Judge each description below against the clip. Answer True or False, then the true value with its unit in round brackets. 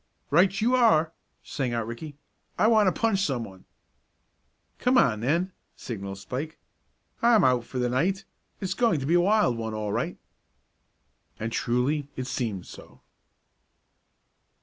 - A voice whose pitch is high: False (140 Hz)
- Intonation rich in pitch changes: True (8.4 semitones)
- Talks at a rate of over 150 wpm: False (145 wpm)